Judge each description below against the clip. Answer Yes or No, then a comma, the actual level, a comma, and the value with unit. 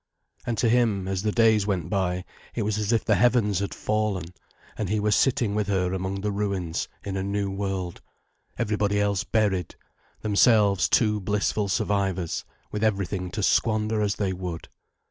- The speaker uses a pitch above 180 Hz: No, low, 100 Hz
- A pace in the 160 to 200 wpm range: Yes, average, 170 wpm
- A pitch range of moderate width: No, narrow, 2.0 semitones